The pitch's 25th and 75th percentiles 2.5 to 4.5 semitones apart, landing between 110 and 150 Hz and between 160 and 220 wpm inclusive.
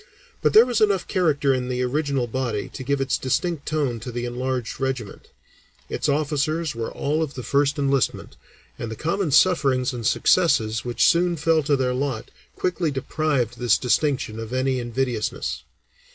Yes: average, 3.9 semitones; low, 135 Hz; average, 165 wpm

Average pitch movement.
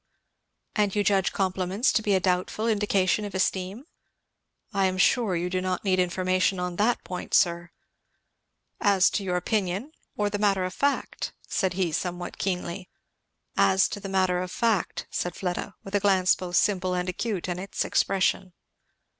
No: narrow, 2.0 semitones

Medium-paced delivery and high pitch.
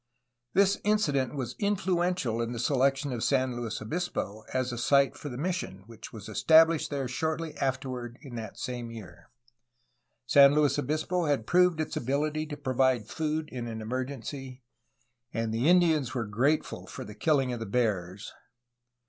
No: average, 165 wpm; low, 135 Hz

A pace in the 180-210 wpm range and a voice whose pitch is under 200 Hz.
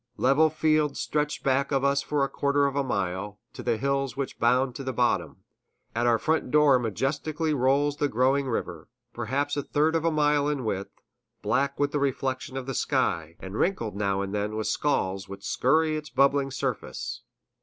Yes: average, 190 wpm; low, 135 Hz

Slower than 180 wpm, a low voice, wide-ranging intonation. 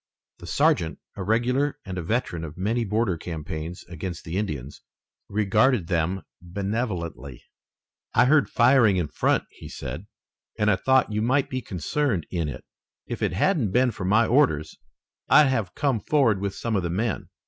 Yes: average, 170 wpm; low, 100 Hz; wide, 5.7 semitones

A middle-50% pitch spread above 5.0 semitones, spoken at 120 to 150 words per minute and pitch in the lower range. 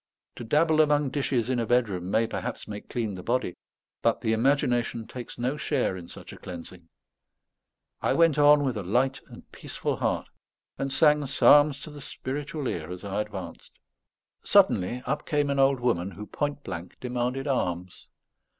No: wide, 5.5 semitones; average, 170 wpm; low, 125 Hz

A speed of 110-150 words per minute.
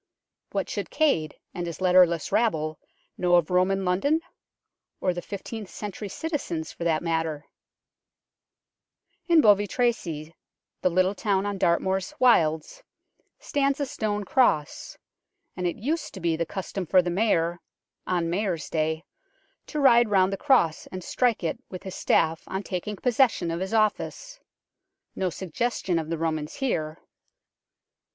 Yes: average, 145 wpm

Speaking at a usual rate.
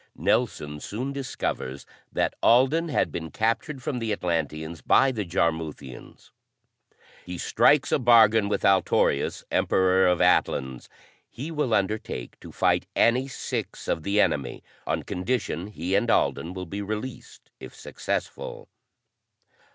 No: slow, 130 wpm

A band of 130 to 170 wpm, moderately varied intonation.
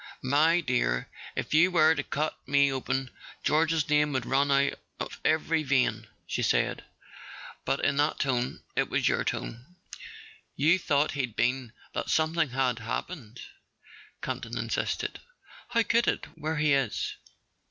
Yes: average, 140 wpm; average, 3.5 semitones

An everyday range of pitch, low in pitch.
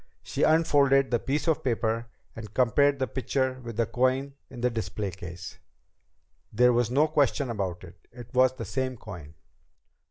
Yes: average, 3.4 semitones; low, 125 Hz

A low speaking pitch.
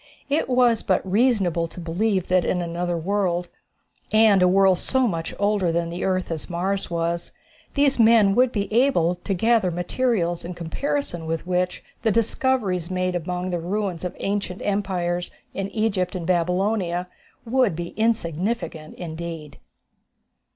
No: medium, 185 Hz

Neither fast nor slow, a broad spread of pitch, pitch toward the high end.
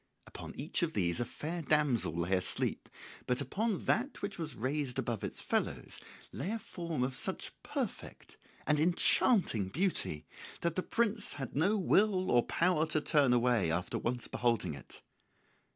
No: average, 160 wpm; wide, 7.1 semitones; medium, 150 Hz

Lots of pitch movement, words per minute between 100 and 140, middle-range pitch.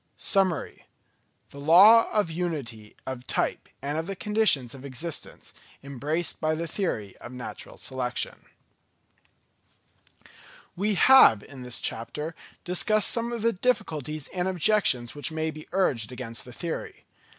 Yes: wide, 6.8 semitones; slow, 135 wpm; medium, 155 Hz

